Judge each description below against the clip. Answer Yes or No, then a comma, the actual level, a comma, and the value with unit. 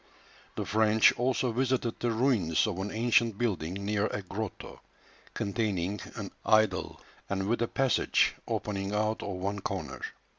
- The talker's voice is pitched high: No, low, 105 Hz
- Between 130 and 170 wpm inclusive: Yes, average, 145 wpm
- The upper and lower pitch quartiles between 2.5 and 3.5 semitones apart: Yes, average, 3.0 semitones